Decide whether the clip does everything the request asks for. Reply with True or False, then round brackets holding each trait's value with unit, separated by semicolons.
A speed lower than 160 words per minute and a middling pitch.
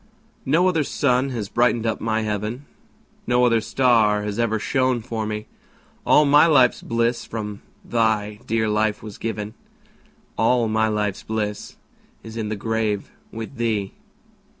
False (150 wpm; 110 Hz)